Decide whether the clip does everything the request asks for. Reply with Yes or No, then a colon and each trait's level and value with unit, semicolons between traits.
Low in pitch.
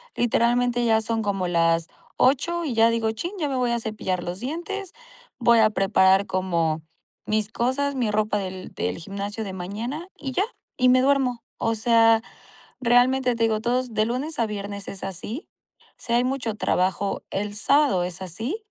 No: high, 225 Hz